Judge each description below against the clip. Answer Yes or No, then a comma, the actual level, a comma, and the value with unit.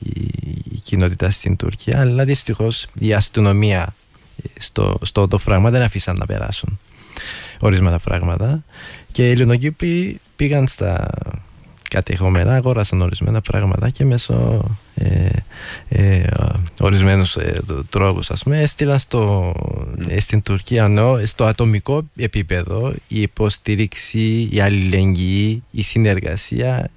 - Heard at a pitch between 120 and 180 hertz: No, low, 105 Hz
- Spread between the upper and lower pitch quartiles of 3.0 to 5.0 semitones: Yes, average, 3.8 semitones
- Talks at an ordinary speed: No, slow, 110 wpm